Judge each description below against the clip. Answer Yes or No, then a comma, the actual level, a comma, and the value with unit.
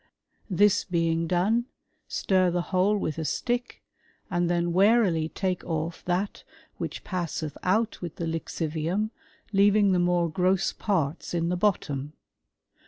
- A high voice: No, medium, 180 Hz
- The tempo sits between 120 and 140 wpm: Yes, slow, 135 wpm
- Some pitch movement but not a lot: Yes, average, 3.1 semitones